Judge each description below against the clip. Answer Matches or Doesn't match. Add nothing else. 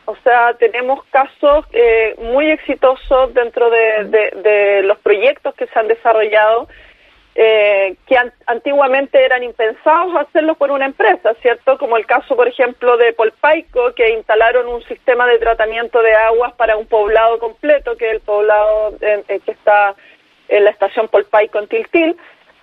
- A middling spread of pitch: Matches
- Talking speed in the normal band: Matches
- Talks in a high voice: Matches